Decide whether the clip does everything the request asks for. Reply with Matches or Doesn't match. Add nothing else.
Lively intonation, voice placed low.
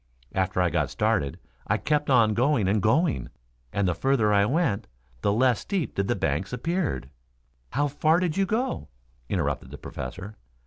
Matches